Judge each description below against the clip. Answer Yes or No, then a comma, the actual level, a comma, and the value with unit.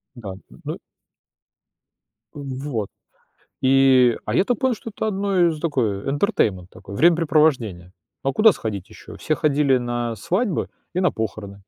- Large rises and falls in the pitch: Yes, wide, 7.4 semitones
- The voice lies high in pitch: No, low, 135 Hz